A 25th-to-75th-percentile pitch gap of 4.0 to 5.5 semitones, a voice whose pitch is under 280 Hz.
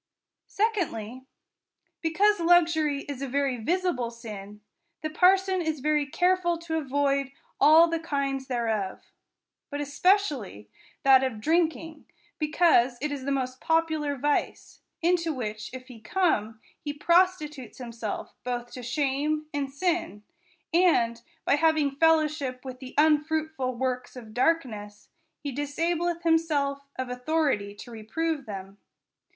No: average, 4.5 semitones; very high, 285 Hz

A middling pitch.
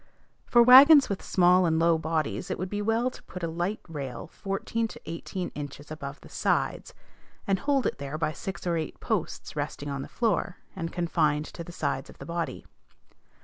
Yes: medium, 170 Hz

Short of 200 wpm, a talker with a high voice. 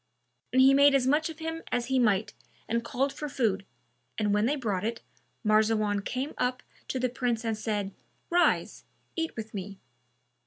Yes: average, 180 wpm; high, 235 Hz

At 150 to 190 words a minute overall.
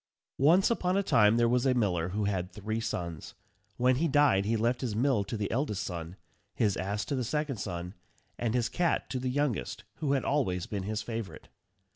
No: fast, 205 wpm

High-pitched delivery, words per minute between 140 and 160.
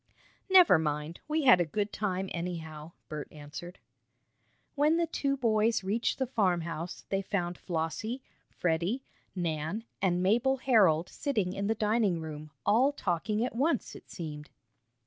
Yes: high, 195 Hz; average, 145 wpm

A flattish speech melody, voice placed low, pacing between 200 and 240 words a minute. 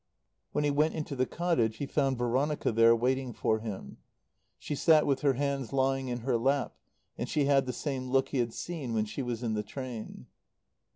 No: average, 3.2 semitones; low, 130 Hz; fast, 205 wpm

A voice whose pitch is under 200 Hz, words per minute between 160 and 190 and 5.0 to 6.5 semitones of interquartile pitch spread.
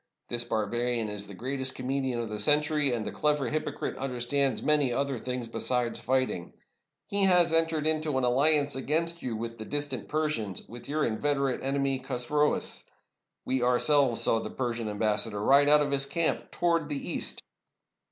No: low, 135 Hz; average, 170 wpm; average, 3.7 semitones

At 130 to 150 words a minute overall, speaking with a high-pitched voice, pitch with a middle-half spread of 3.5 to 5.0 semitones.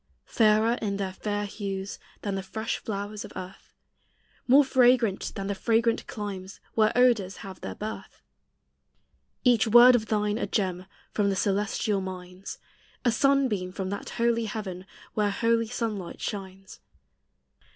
No: average, 140 wpm; high, 210 Hz; average, 2.9 semitones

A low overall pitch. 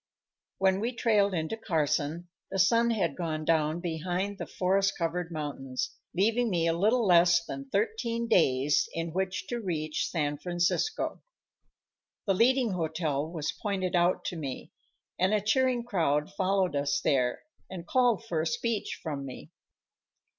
No: medium, 180 Hz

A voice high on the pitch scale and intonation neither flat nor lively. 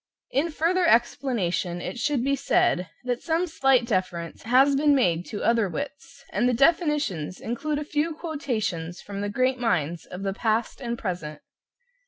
No: high, 240 Hz; wide, 7.3 semitones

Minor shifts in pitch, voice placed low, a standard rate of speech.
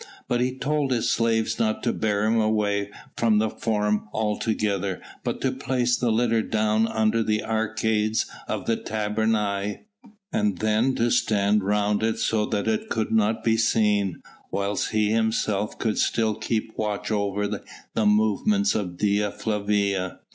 Yes: narrow, 1.4 semitones; low, 110 Hz; average, 155 wpm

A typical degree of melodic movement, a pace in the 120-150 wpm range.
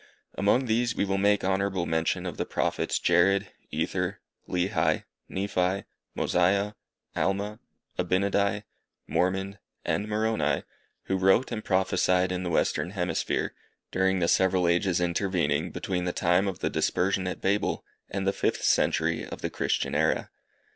No: narrow, 2.0 semitones; average, 140 wpm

